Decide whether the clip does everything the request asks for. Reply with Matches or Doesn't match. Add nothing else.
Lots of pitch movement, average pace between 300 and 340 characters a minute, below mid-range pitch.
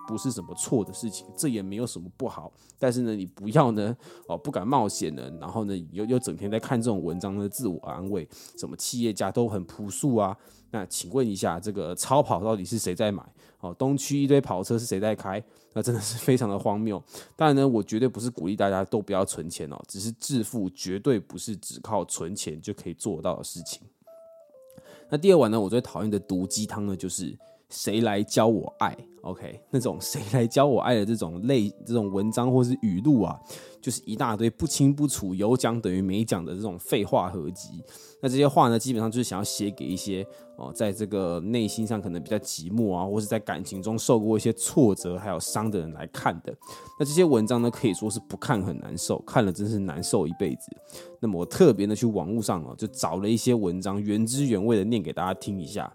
Doesn't match